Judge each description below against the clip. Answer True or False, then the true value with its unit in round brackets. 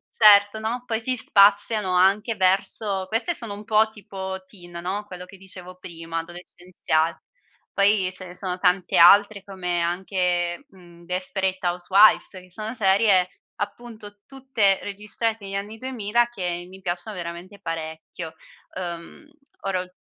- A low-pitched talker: False (190 Hz)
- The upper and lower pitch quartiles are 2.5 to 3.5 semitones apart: True (2.8 semitones)